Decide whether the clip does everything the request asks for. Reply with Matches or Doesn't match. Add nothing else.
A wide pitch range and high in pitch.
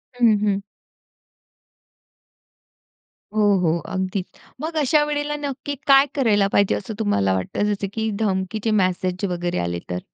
Matches